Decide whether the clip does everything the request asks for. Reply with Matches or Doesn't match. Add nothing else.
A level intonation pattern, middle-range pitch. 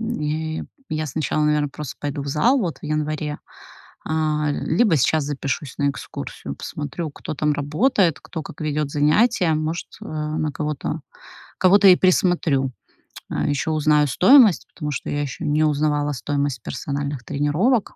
Matches